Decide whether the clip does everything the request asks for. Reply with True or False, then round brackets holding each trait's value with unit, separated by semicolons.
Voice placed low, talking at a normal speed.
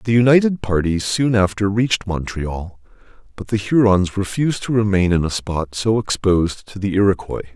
True (100 Hz; 165 wpm)